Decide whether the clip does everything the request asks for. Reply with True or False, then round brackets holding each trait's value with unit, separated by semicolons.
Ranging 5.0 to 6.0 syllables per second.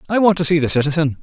False (7.8 syllables/s)